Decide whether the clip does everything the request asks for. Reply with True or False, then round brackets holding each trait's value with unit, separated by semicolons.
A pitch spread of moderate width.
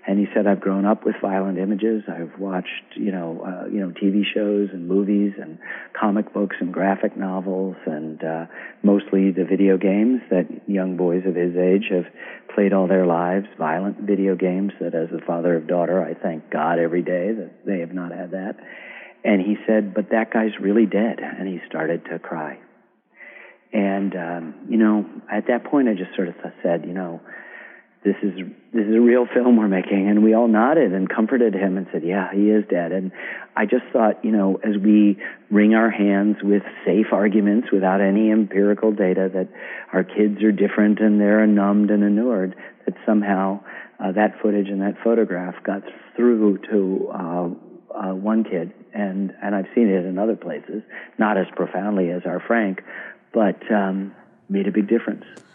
False (2.1 semitones)